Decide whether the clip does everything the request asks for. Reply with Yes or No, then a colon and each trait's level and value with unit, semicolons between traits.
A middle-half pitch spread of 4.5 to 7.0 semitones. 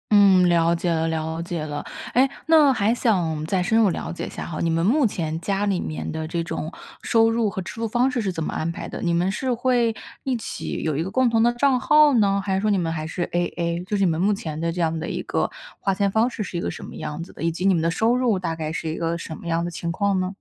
Yes: average, 5.1 semitones